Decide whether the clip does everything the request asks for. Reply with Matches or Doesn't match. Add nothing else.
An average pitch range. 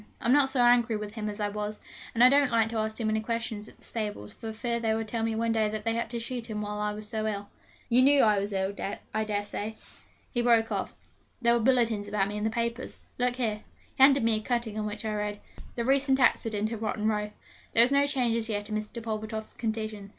Doesn't match